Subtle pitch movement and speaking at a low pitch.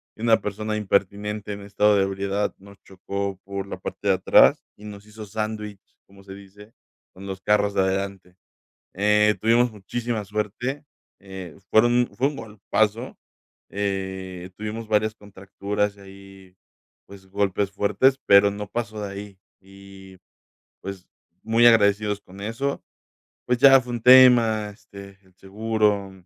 Yes: narrow, 1.9 semitones; low, 100 Hz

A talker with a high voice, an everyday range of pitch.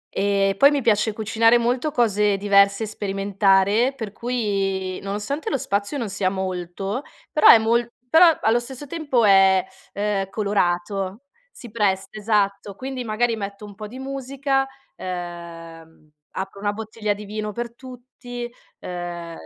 Yes: high, 210 Hz; average, 3.7 semitones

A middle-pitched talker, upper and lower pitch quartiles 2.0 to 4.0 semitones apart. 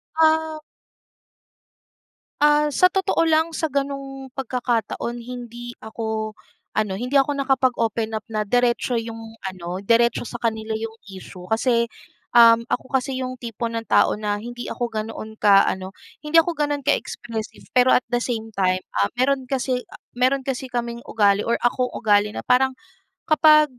No: high, 240 Hz; average, 3.4 semitones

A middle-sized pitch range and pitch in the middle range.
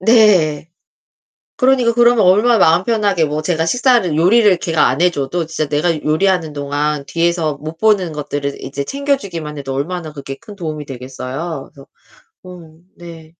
Yes: average, 4.5 semitones; medium, 165 Hz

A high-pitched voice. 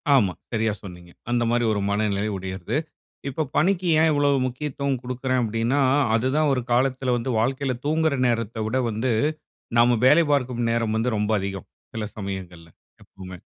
No: low, 120 Hz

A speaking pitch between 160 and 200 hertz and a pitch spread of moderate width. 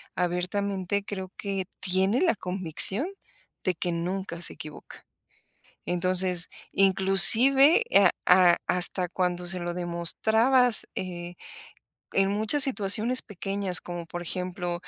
No: medium, 185 Hz; narrow, 2.3 semitones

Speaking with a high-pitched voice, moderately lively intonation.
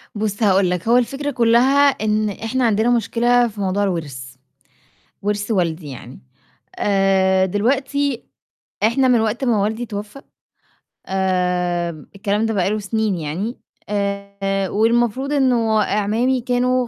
Yes: high, 210 Hz; average, 3.7 semitones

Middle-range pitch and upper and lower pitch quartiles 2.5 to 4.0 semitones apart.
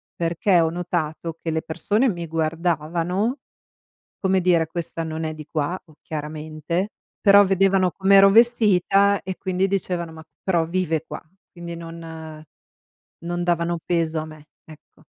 Yes: medium, 170 Hz; average, 2.8 semitones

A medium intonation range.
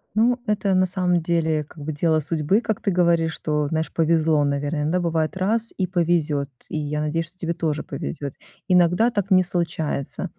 Yes: average, 3.1 semitones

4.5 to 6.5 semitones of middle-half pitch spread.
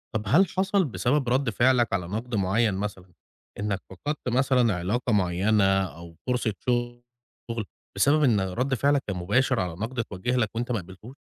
Yes: average, 4.8 semitones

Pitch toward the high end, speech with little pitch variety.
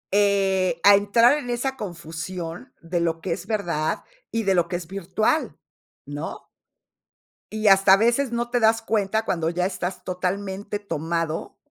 No: high, 195 Hz; average, 4.2 semitones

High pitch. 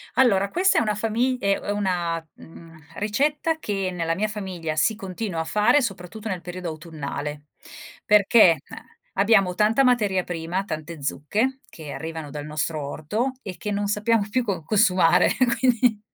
Yes: high, 195 Hz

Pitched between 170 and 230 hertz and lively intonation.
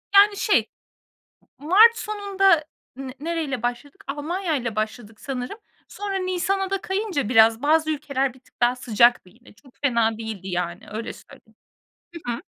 No: very high, 275 Hz; wide, 8.1 semitones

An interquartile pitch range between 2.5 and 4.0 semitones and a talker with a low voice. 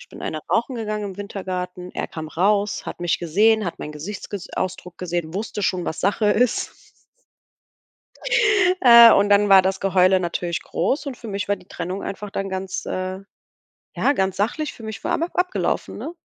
No: average, 2.8 semitones; high, 195 Hz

